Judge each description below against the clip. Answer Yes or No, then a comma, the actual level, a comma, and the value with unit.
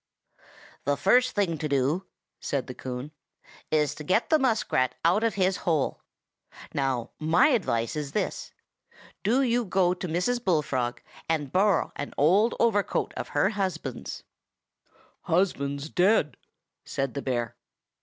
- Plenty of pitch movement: Yes, wide, 6.3 semitones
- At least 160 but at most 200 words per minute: No, slow, 135 wpm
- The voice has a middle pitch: Yes, medium, 165 Hz